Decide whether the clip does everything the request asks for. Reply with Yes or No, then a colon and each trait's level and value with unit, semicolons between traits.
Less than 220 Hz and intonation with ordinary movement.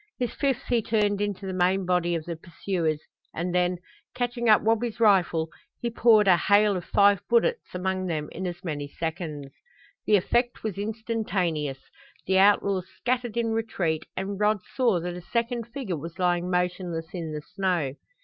Yes: high, 190 Hz; average, 4.2 semitones